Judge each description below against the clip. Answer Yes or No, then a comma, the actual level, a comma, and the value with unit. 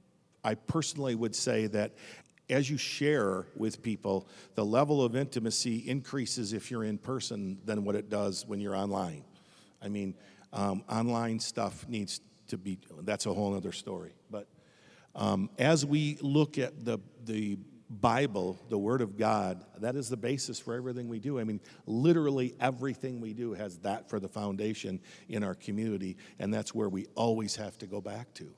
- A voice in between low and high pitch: No, low, 115 Hz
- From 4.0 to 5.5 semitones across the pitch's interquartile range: Yes, average, 4.4 semitones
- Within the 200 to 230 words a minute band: No, average, 175 wpm